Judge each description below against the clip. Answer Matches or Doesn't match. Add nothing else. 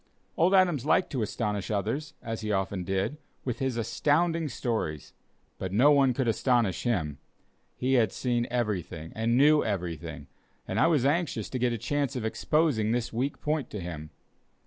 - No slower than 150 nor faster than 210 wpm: Matches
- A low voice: Matches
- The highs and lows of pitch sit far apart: Matches